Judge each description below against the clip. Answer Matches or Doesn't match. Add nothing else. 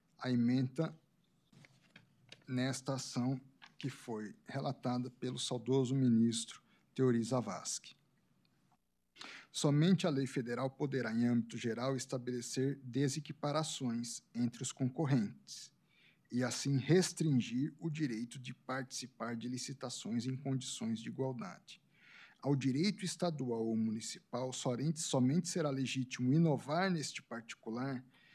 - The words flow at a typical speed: Doesn't match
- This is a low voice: Matches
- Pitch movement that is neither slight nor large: Matches